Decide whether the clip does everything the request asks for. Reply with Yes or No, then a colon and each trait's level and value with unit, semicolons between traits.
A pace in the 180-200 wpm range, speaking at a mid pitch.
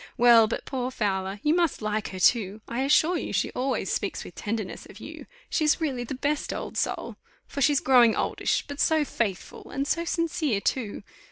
No: average, 195 wpm; very high, 255 Hz